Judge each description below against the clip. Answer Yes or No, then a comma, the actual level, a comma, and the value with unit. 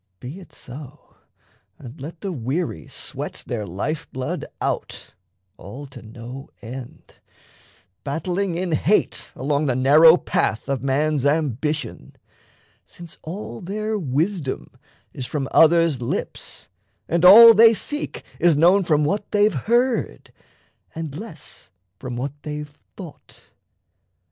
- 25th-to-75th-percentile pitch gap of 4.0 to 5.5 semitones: Yes, average, 5.2 semitones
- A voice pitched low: No, medium, 150 Hz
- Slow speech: Yes, slow, 125 wpm